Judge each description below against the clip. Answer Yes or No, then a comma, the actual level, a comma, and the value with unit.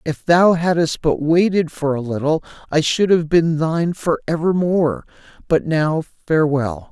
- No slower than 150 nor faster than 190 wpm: Yes, average, 165 wpm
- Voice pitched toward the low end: No, medium, 160 Hz